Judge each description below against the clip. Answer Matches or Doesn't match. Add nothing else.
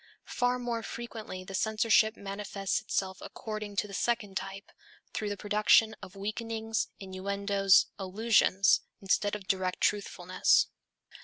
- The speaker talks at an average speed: Doesn't match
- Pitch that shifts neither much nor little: Doesn't match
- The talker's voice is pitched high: Matches